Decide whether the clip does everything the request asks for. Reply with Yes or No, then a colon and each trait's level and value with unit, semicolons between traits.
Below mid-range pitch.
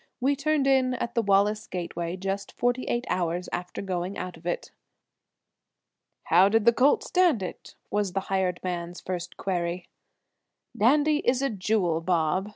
No: high, 195 Hz